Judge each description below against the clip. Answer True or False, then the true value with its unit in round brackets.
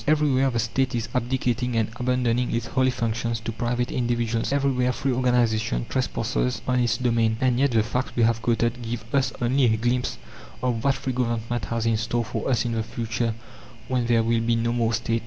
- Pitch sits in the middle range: False (120 Hz)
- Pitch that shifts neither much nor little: False (1.6 semitones)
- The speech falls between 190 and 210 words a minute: True (200 wpm)